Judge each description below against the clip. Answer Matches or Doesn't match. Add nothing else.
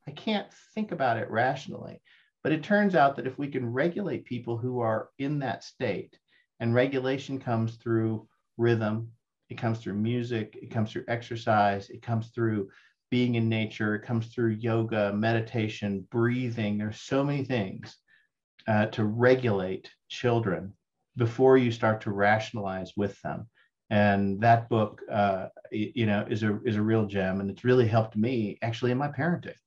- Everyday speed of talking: Matches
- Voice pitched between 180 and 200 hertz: Doesn't match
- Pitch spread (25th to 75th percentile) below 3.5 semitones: Matches